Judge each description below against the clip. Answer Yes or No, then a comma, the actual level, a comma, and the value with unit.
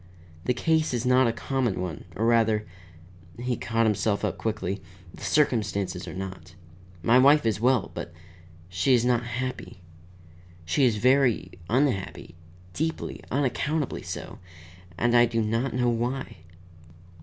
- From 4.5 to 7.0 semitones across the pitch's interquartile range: No, average, 3.7 semitones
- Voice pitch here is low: Yes, low, 120 Hz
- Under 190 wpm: Yes, average, 140 wpm